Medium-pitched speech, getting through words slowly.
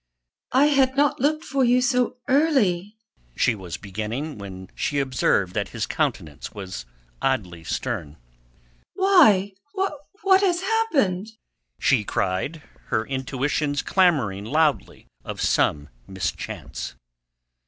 Yes: medium, 150 Hz; slow, 110 wpm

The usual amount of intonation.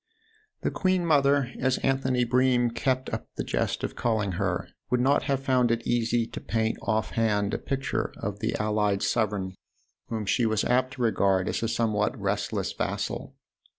Yes: average, 3.2 semitones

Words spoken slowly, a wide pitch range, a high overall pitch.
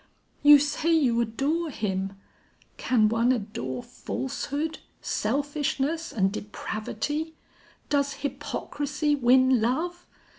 No: slow, 90 wpm; average, 4.7 semitones; very high, 275 Hz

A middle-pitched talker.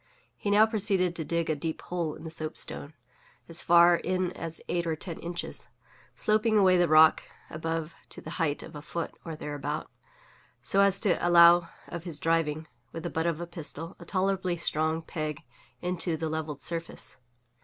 Yes: medium, 170 Hz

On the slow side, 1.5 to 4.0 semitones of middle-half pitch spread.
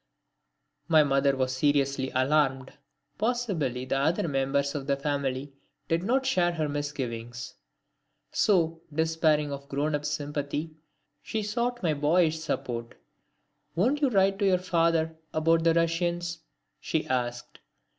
Yes: slow, 130 wpm; average, 3.7 semitones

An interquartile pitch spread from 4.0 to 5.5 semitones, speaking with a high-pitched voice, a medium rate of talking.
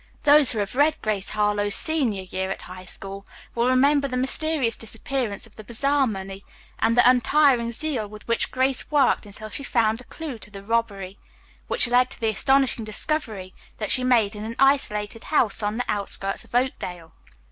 Yes: average, 4.4 semitones; high, 230 Hz; average, 185 wpm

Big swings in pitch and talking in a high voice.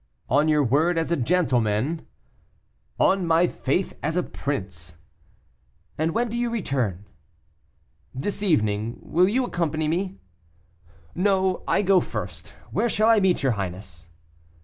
No: wide, 7.8 semitones; medium, 160 Hz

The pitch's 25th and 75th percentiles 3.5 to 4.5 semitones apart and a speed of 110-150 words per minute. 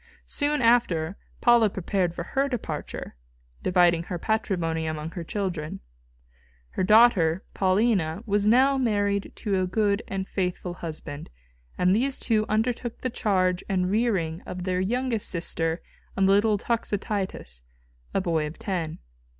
Yes: average, 4.2 semitones; average, 140 wpm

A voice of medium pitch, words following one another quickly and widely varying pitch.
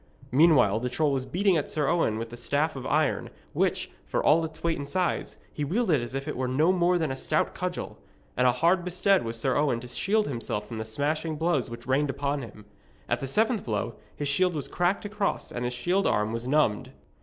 Yes: medium, 145 Hz; fast, 225 wpm; wide, 5.7 semitones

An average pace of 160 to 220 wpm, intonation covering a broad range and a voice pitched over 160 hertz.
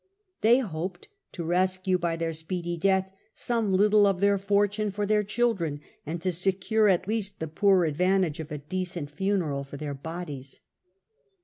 No: average, 165 wpm; average, 3.7 semitones; medium, 185 Hz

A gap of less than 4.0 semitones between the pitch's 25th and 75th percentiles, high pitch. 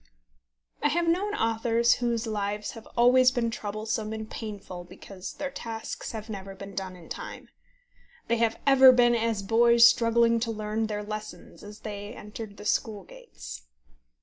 Yes: narrow, 2.4 semitones; high, 220 Hz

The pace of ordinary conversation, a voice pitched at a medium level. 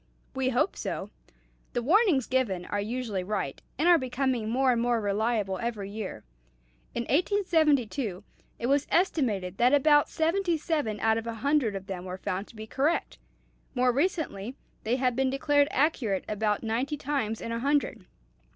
No: average, 165 wpm; high, 245 Hz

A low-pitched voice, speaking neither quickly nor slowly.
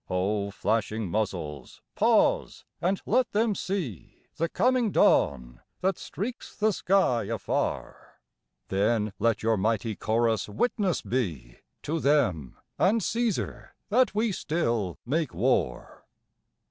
No: low, 115 Hz; slow, 115 wpm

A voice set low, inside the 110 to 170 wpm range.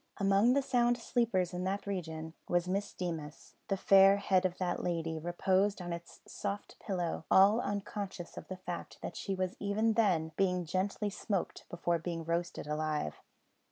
No: medium, 185 Hz; average, 165 wpm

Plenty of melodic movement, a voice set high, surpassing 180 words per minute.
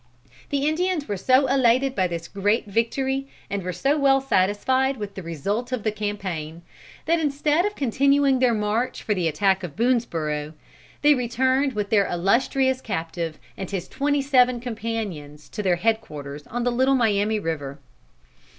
No: wide, 6.0 semitones; high, 225 Hz; average, 165 wpm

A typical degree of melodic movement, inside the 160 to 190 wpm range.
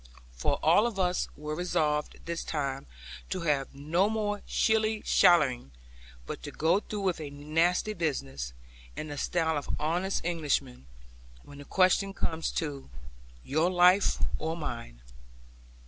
No: average, 4.2 semitones; average, 140 wpm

